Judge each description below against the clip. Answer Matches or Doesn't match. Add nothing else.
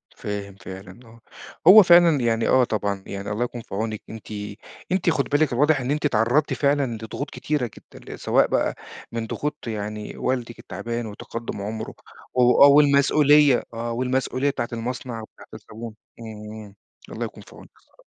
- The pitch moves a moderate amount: Matches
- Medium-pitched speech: Doesn't match